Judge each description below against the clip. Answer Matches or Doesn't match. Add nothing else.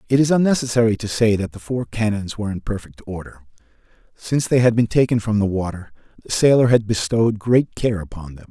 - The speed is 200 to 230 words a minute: Matches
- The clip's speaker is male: Matches